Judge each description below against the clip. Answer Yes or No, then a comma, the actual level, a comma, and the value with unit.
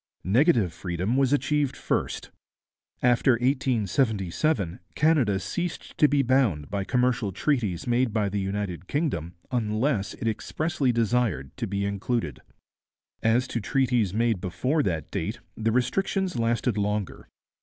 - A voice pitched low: Yes, low, 115 Hz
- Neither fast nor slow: No, slow, 130 wpm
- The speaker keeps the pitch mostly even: No, average, 4.8 semitones